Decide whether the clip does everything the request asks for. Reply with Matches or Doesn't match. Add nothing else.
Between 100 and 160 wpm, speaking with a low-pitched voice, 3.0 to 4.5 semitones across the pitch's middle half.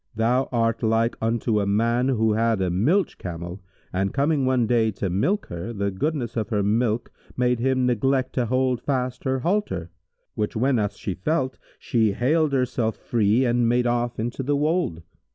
Doesn't match